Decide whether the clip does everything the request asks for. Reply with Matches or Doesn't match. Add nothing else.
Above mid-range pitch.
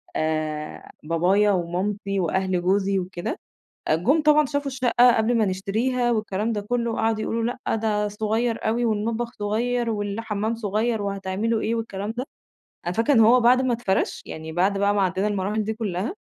Matches